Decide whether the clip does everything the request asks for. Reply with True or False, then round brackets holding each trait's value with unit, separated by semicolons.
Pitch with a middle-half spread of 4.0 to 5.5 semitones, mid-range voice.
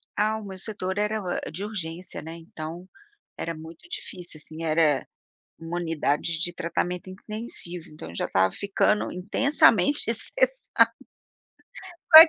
True (4.5 semitones; 180 Hz)